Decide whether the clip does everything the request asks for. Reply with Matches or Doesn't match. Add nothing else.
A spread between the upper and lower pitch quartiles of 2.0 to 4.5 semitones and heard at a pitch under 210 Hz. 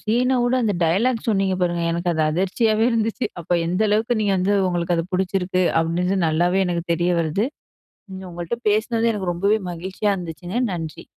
Matches